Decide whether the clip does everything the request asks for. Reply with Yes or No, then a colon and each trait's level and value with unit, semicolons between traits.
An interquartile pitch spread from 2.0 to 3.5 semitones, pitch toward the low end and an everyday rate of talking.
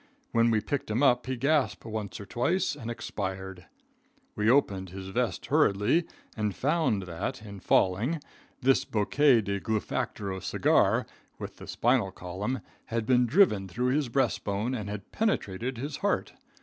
No: average, 4.9 semitones; low, 115 Hz; average, 155 wpm